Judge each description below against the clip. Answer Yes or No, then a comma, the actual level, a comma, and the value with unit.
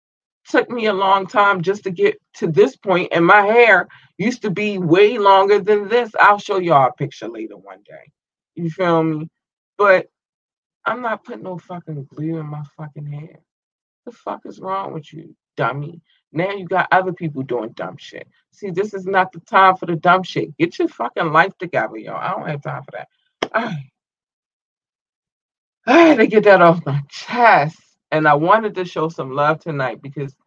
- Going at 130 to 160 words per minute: No, average, 190 wpm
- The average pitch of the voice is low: No, medium, 185 Hz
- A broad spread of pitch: No, average, 4.7 semitones